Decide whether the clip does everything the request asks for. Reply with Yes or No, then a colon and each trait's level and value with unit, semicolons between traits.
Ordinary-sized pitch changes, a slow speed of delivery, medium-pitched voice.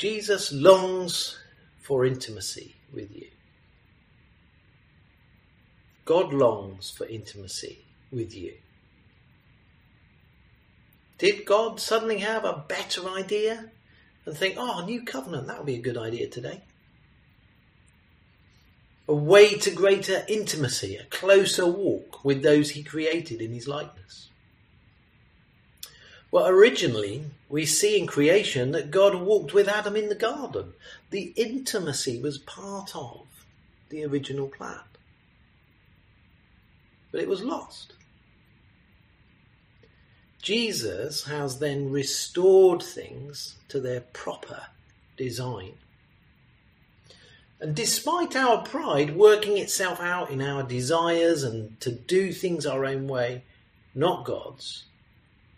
No: wide, 7.1 semitones; slow, 110 wpm; medium, 160 Hz